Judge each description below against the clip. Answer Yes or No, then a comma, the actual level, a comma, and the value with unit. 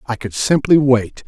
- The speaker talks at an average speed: Yes, average, 190 wpm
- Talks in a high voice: No, low, 120 Hz